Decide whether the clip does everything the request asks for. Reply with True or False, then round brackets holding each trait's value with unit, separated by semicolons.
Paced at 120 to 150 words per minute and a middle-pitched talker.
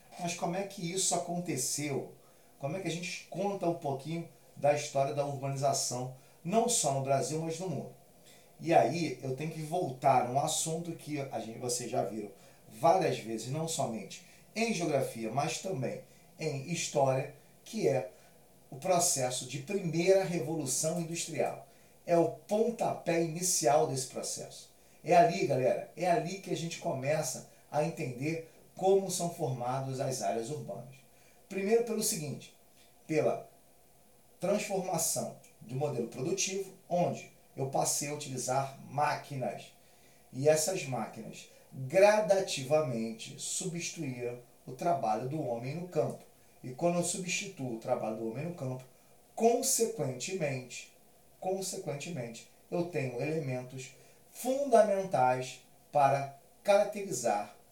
True (130 wpm; 160 Hz)